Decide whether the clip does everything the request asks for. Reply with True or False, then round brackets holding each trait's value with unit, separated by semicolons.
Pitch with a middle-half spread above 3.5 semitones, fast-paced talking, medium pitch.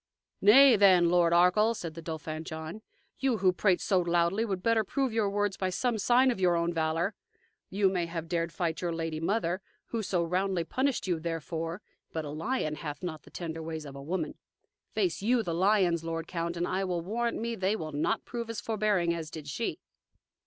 True (4.1 semitones; 210 wpm; 180 Hz)